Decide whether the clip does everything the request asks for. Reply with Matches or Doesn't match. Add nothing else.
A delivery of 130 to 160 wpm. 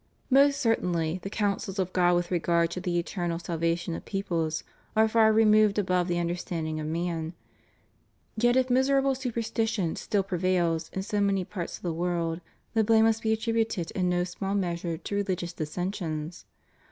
Doesn't match